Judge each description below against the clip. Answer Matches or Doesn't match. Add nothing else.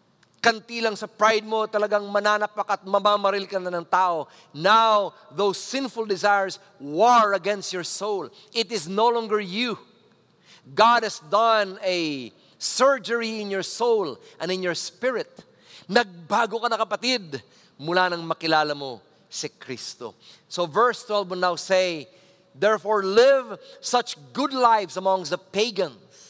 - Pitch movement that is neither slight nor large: Matches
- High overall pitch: Matches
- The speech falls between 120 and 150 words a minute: Matches